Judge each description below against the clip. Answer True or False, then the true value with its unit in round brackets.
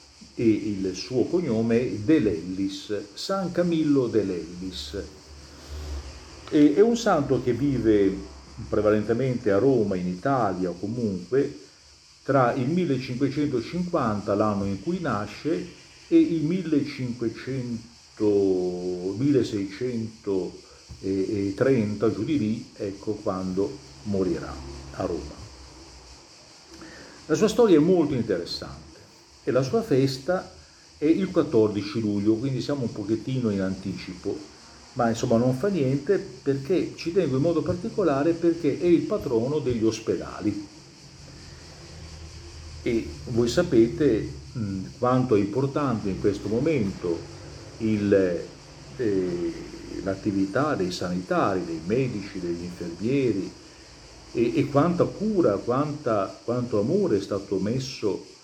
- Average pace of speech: False (110 wpm)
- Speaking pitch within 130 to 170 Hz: False (115 Hz)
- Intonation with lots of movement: True (6.5 semitones)